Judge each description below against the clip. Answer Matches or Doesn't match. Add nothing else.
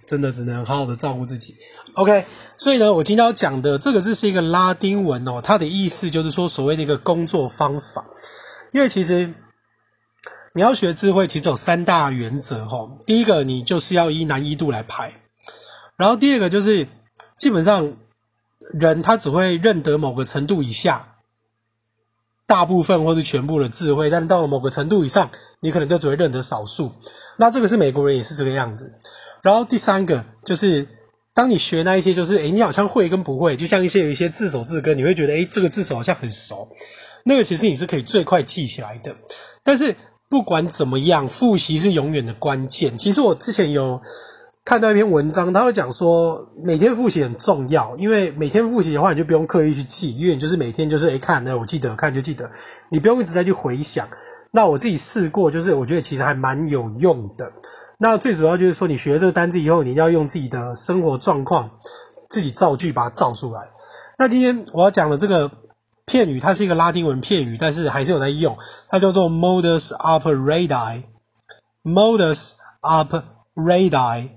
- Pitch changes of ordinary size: Doesn't match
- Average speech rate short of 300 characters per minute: Doesn't match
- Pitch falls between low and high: Matches